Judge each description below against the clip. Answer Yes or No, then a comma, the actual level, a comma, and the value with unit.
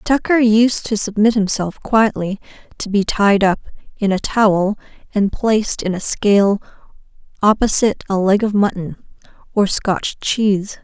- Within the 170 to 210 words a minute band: No, average, 145 wpm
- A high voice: Yes, high, 205 Hz